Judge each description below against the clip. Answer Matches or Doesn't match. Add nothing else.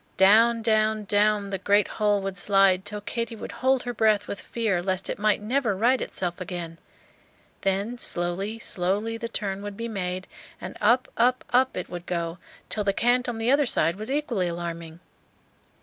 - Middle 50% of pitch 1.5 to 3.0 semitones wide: Doesn't match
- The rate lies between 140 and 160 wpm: Doesn't match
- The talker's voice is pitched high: Matches